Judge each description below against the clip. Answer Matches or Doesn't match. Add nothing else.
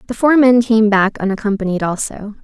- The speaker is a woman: Matches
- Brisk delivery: Doesn't match